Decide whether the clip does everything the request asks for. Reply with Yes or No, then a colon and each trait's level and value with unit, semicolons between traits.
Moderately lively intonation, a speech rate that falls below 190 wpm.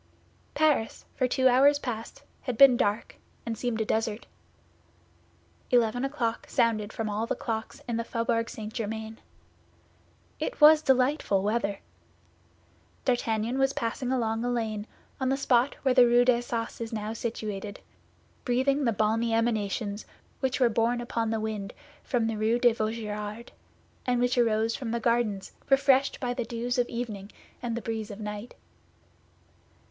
No: narrow, 2.1 semitones; average, 150 wpm